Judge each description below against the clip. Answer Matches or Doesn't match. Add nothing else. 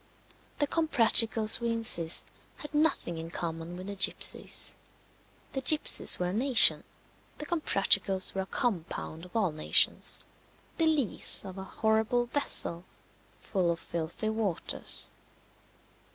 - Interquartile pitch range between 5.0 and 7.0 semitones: Matches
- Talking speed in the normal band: Doesn't match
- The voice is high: Matches